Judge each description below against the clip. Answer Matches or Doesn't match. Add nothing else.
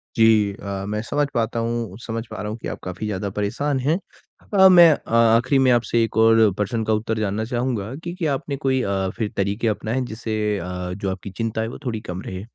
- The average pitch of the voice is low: Matches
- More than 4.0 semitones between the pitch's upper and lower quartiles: Doesn't match